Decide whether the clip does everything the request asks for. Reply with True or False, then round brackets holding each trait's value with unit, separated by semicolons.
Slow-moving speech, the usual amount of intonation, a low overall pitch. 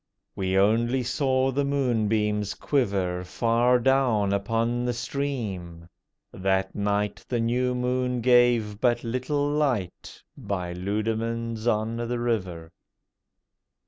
True (110 wpm; 3.7 semitones; 115 Hz)